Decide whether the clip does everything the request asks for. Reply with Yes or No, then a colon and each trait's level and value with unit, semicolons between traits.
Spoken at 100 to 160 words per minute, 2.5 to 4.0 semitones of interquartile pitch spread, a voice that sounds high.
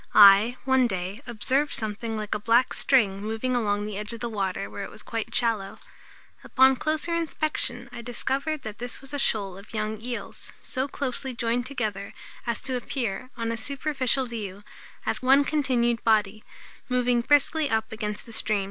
No: average, 175 wpm; average, 3.6 semitones; high, 235 Hz